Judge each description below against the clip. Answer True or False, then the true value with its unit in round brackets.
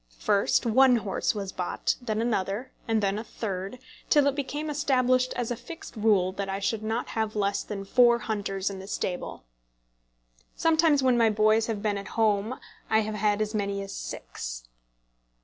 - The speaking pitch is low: False (215 Hz)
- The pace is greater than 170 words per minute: True (180 wpm)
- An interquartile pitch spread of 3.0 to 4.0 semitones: True (3.6 semitones)